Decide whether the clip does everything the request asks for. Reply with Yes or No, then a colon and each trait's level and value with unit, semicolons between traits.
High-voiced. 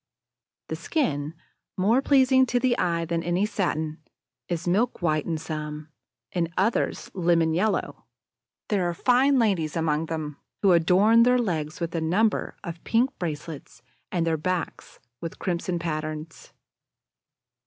No: medium, 170 Hz